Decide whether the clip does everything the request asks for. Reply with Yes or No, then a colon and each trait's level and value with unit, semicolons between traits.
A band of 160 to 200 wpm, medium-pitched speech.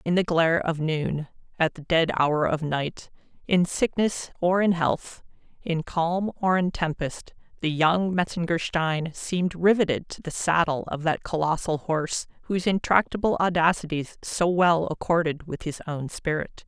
No: average, 140 wpm; medium, 165 Hz